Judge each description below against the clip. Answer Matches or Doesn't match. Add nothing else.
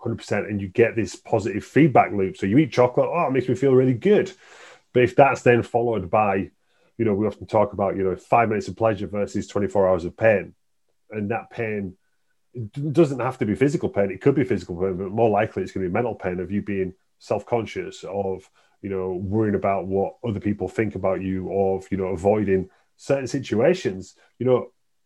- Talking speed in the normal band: Doesn't match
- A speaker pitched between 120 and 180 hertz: Doesn't match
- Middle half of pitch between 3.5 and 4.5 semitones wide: Matches